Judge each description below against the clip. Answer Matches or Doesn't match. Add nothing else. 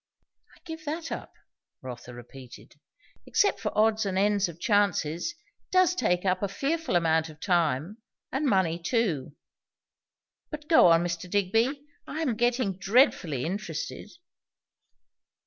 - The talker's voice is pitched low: Doesn't match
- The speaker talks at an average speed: Doesn't match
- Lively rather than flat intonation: Matches